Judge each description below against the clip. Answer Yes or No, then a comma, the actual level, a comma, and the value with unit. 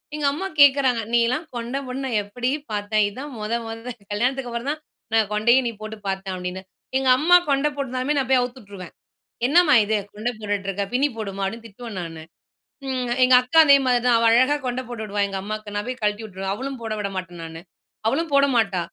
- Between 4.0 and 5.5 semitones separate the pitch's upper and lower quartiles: Yes, average, 4.3 semitones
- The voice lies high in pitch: Yes, high, 235 Hz